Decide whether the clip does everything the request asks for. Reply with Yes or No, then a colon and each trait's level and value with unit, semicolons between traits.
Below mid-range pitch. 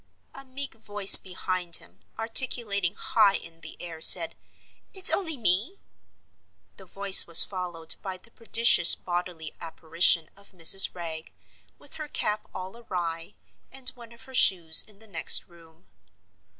No: medium, 185 Hz